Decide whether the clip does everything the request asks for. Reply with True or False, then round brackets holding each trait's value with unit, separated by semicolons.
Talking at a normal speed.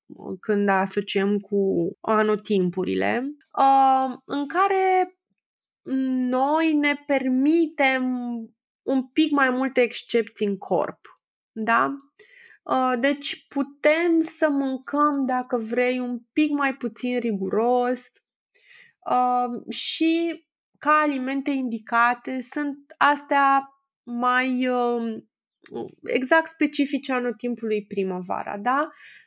False (80 wpm)